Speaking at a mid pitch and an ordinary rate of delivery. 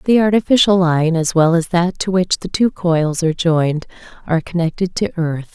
Yes: medium, 175 Hz; average, 195 wpm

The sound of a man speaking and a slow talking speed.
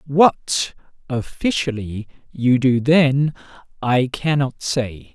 Yes: male; slow, 70 wpm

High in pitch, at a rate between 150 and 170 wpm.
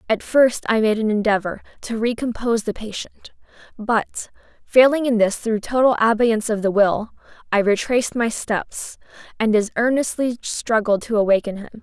Yes: high, 225 Hz; average, 160 wpm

